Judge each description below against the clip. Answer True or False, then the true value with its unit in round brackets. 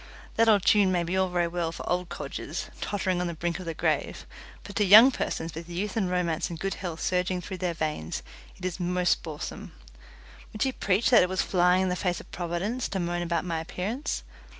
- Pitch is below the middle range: False (180 Hz)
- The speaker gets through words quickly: True (220 wpm)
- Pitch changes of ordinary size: False (2.0 semitones)